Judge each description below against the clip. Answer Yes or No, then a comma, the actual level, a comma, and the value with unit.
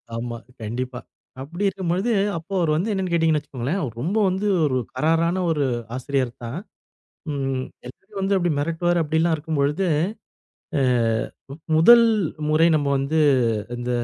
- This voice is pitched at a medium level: Yes, medium, 160 Hz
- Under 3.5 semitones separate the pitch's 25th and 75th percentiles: No, average, 4.5 semitones